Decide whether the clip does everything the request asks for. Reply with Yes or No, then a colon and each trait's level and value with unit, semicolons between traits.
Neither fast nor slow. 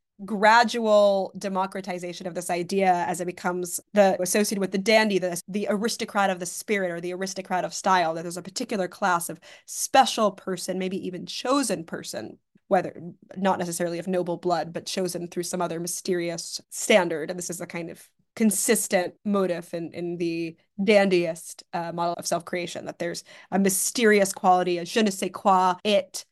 Yes: average, 175 wpm